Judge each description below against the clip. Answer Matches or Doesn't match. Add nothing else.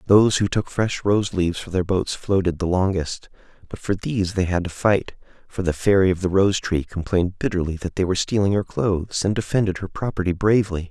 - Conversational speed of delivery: Doesn't match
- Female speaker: Doesn't match